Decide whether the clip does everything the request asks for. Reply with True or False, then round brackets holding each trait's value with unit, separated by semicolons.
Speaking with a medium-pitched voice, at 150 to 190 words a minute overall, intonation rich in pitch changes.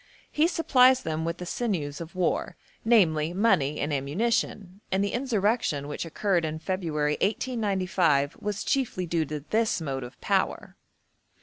False (180 Hz; 140 wpm; 6.2 semitones)